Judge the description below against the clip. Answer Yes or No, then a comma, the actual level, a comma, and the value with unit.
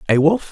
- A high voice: No, medium, 170 Hz